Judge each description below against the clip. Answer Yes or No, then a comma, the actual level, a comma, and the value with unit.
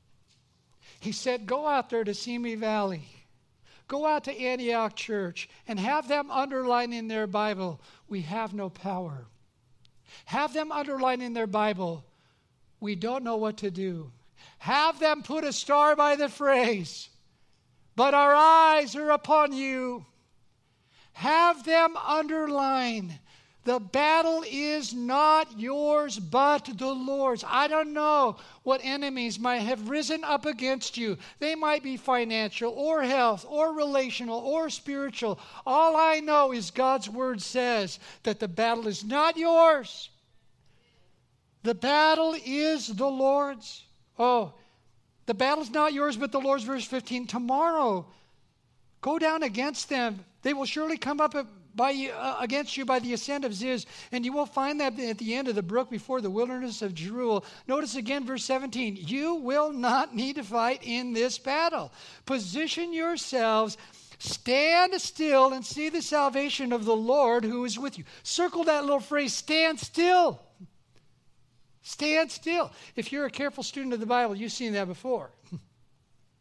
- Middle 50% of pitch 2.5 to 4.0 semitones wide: No, average, 5.1 semitones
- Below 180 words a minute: Yes, average, 150 wpm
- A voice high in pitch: Yes, very high, 255 Hz